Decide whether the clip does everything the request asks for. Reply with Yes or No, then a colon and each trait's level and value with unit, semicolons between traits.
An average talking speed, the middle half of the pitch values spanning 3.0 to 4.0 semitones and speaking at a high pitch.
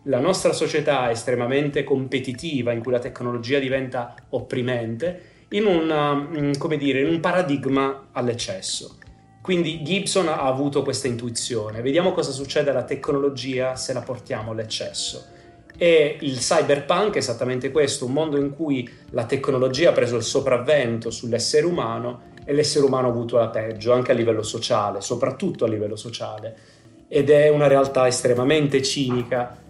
No: average, 150 wpm; average, 3.3 semitones; low, 135 Hz